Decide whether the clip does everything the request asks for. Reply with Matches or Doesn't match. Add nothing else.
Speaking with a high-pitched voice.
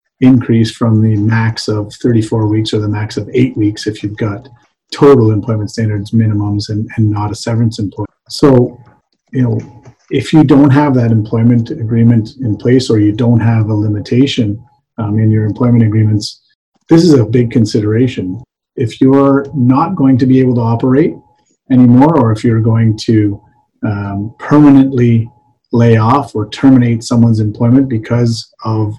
Doesn't match